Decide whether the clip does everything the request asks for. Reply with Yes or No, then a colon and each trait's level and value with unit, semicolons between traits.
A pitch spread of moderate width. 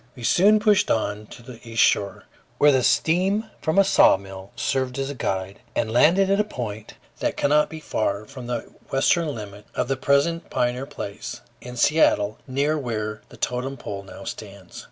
No: wide, 6.1 semitones